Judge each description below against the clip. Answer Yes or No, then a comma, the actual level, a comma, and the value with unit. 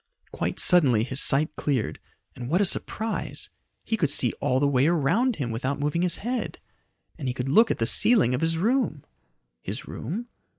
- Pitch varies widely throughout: Yes, wide, 7.6 semitones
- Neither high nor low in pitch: Yes, medium, 150 Hz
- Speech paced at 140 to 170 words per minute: No, average, 185 wpm